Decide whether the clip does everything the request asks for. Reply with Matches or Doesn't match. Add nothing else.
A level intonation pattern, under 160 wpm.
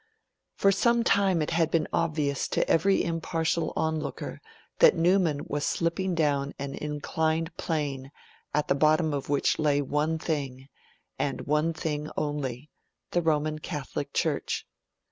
Matches